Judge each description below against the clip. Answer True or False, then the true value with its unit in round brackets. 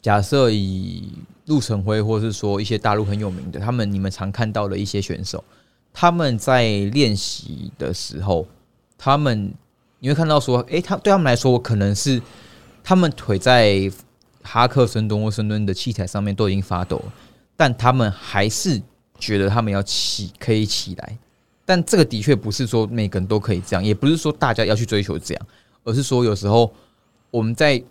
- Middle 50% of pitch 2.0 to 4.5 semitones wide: True (3.7 semitones)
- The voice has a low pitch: True (110 Hz)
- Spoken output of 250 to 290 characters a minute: True (275 characters per minute)